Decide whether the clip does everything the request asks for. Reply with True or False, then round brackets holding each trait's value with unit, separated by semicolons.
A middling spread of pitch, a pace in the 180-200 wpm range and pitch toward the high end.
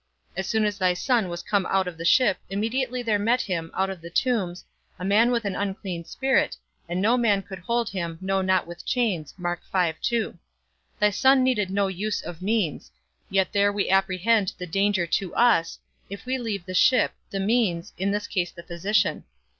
True (3.7 semitones; 190 wpm; 195 Hz)